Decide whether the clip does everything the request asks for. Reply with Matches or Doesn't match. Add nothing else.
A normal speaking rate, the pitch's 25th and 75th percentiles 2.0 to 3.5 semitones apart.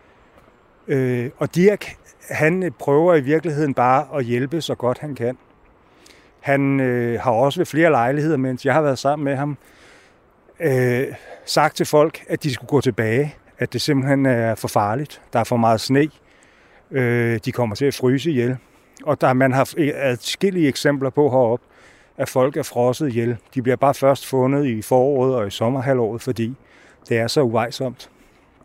Matches